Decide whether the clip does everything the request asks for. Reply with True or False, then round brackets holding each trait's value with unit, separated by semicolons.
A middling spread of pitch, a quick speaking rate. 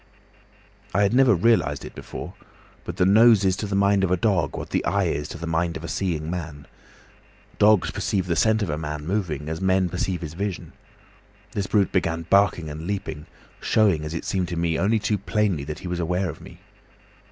True (3.7 semitones; 210 wpm)